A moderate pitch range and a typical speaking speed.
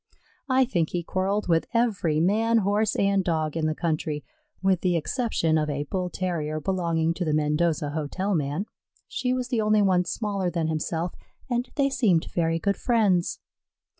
Yes: average, 4.5 semitones; average, 170 wpm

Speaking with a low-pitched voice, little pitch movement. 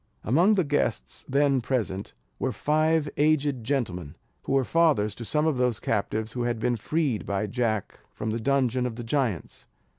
No: low, 125 Hz; average, 4.8 semitones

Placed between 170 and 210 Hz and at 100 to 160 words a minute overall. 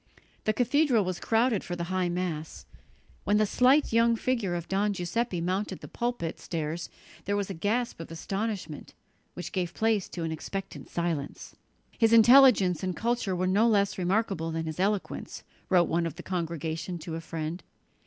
No: medium, 185 Hz; average, 175 wpm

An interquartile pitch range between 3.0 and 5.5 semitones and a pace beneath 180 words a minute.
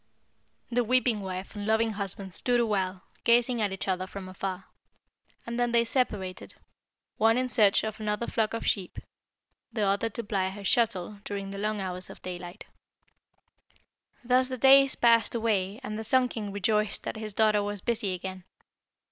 Yes: average, 3.3 semitones; average, 170 wpm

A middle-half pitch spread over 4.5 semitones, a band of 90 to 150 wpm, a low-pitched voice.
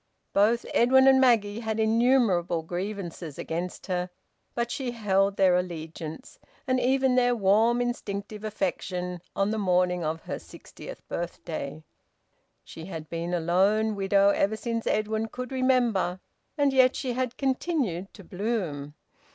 No: average, 5.2 semitones; average, 140 wpm; high, 205 Hz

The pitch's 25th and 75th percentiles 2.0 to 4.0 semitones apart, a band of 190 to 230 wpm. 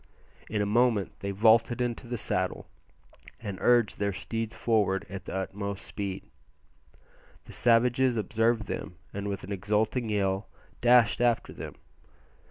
No: average, 3.0 semitones; average, 140 wpm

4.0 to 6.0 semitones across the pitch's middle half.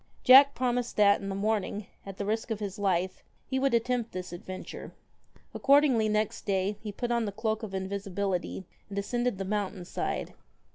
No: average, 3.4 semitones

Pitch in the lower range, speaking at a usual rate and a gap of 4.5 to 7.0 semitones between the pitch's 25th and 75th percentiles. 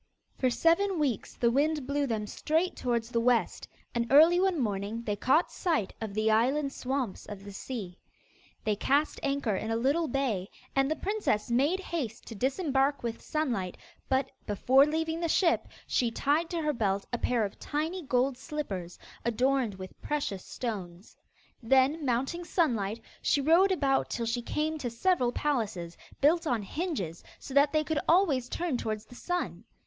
No: very high, 265 Hz; average, 170 wpm; wide, 5.4 semitones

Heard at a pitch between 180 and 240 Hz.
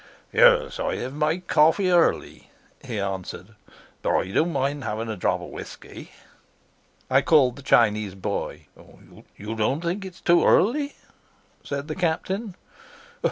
No: medium, 145 Hz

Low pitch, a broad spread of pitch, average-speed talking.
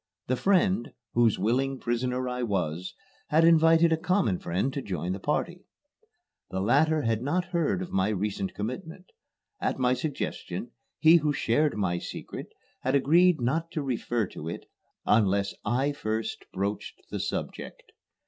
Yes: low, 125 Hz; wide, 7.2 semitones; average, 150 wpm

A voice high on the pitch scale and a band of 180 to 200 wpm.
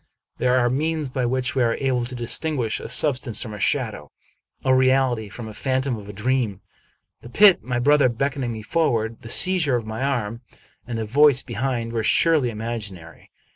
No: low, 125 Hz; average, 195 wpm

